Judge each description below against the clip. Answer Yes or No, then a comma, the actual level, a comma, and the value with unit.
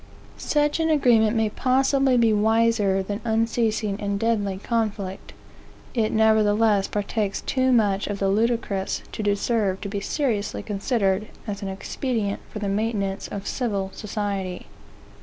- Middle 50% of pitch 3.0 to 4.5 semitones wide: No, narrow, 2.5 semitones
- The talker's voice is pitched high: Yes, high, 215 Hz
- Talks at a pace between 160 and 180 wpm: No, average, 140 wpm